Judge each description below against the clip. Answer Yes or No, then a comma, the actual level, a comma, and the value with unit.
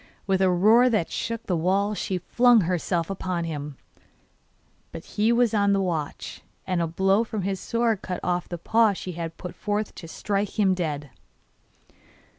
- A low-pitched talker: No, high, 190 Hz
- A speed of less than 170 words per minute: No, average, 175 wpm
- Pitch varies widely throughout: No, average, 3.5 semitones